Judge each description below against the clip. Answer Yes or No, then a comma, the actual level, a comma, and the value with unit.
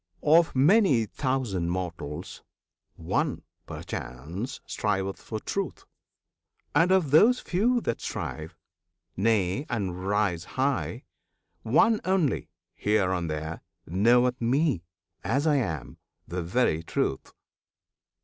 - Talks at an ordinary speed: No, slow, 105 wpm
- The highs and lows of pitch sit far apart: Yes, wide, 8.4 semitones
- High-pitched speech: No, low, 115 Hz